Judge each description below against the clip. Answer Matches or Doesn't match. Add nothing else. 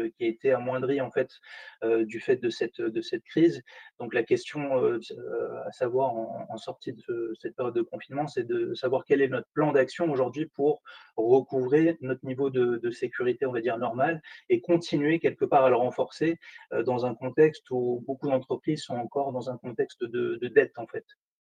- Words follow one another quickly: Doesn't match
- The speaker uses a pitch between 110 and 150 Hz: Doesn't match